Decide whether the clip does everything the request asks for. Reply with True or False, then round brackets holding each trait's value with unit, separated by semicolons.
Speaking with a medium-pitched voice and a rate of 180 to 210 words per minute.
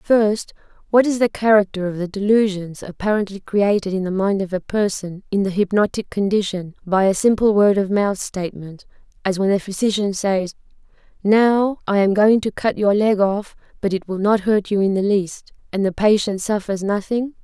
False (200 Hz; 190 wpm)